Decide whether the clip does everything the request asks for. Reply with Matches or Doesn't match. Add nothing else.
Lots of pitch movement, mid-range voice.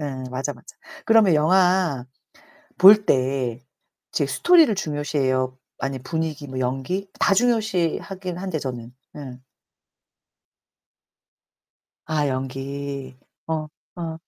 Matches